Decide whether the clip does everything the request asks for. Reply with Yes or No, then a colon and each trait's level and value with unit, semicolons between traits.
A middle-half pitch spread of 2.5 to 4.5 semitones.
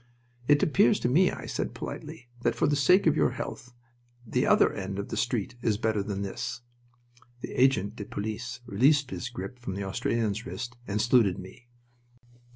Yes: average, 4.0 semitones